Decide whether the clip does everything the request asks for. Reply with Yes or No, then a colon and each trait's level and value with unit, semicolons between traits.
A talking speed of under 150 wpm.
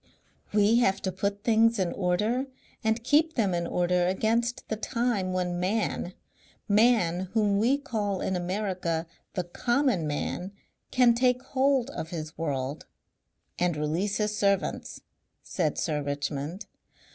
Yes: average, 140 wpm